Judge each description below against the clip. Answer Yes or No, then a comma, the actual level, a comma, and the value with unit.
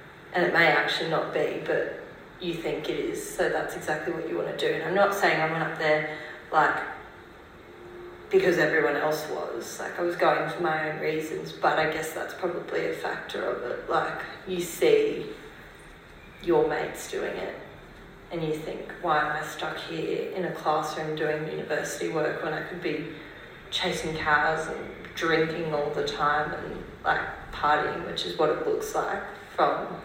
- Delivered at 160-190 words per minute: Yes, average, 180 wpm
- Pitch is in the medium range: Yes, medium, 175 Hz